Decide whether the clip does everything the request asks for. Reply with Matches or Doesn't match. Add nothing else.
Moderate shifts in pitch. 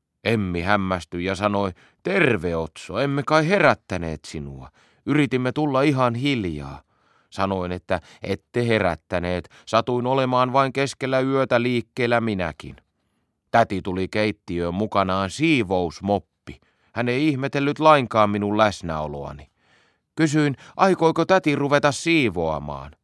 Doesn't match